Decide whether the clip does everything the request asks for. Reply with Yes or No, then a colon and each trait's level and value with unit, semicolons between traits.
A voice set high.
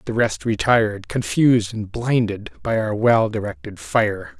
No: low, 110 Hz